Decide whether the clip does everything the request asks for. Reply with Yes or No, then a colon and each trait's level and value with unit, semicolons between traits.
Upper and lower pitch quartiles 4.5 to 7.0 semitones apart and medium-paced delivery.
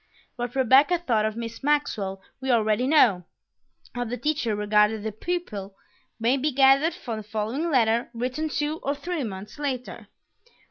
Yes: average, 5.0 semitones; average, 155 wpm